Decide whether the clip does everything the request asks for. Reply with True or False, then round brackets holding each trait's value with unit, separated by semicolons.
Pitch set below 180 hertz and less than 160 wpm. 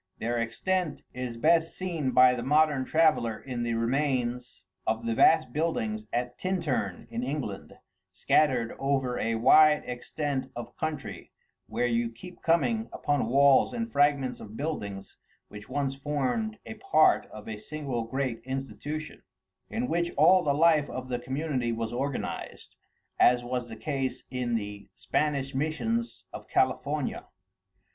True (135 Hz; 145 wpm)